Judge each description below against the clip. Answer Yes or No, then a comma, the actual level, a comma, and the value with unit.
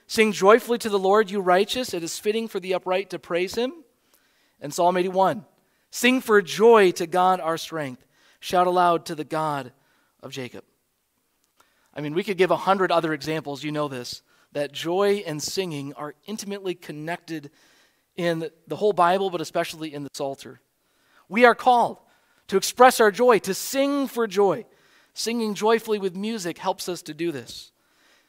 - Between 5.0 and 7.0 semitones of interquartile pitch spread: Yes, wide, 5.6 semitones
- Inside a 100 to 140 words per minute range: No, average, 170 wpm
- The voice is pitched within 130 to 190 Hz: Yes, medium, 185 Hz